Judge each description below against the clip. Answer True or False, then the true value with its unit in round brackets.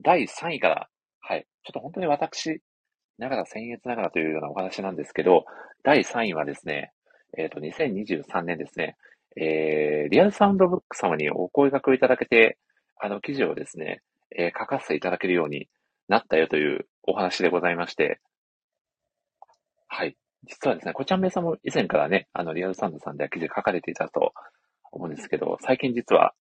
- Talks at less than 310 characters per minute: False (375 characters per minute)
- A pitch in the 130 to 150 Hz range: False (120 Hz)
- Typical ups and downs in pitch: False (9.0 semitones)